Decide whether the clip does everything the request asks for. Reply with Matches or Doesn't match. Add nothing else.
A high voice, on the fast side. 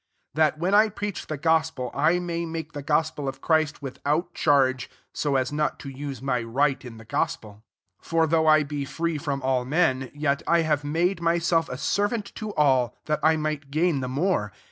Doesn't match